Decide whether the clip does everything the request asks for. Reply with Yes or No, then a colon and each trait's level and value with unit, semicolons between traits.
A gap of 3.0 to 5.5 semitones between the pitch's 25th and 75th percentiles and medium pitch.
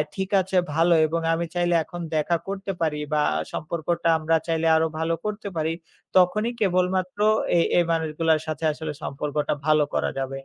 No: narrow, 2.6 semitones; medium, 165 Hz